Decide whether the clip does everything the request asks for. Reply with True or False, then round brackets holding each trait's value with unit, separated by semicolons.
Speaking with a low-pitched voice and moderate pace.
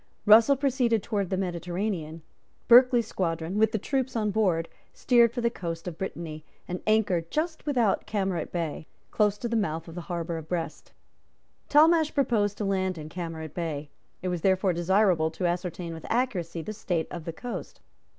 False (190 Hz; 175 wpm)